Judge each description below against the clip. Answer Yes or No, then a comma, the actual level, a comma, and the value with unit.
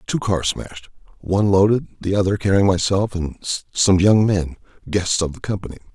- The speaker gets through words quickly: No, average, 170 wpm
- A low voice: Yes, very low, 95 Hz